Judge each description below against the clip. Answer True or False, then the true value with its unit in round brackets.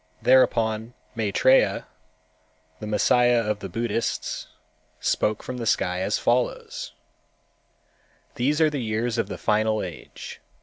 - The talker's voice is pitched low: True (115 Hz)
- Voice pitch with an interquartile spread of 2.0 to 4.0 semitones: True (2.9 semitones)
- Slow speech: True (120 wpm)